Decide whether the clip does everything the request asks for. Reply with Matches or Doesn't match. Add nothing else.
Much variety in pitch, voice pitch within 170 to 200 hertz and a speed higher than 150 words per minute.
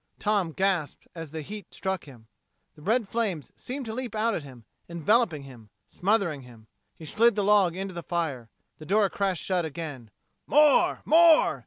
Matches